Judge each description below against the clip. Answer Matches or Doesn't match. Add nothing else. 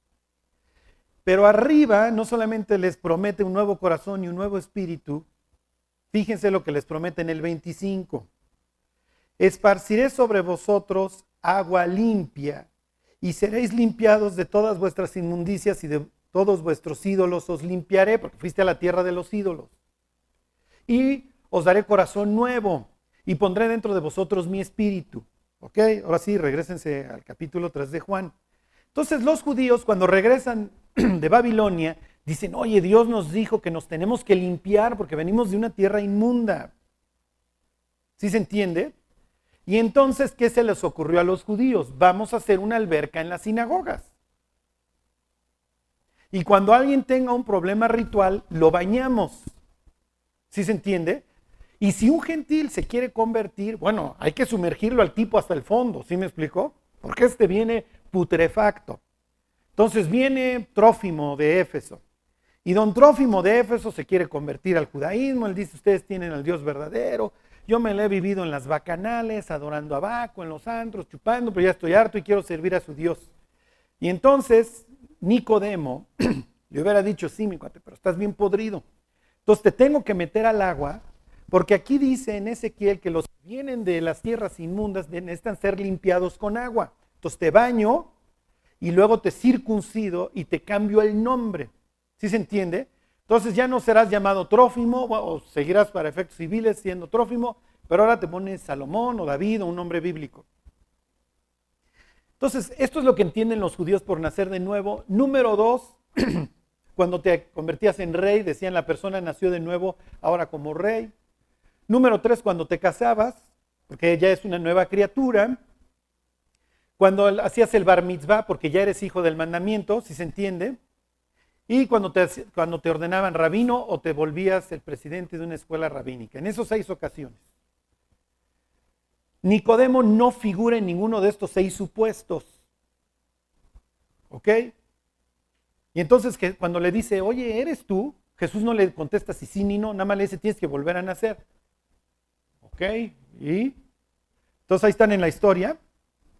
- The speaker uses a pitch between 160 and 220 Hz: Matches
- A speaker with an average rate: Matches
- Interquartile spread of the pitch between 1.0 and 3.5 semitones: Doesn't match